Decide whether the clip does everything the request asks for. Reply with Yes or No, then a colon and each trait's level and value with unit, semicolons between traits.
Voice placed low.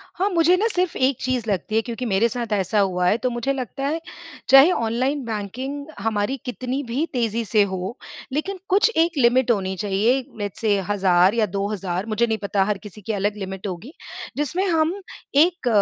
No: high, 230 Hz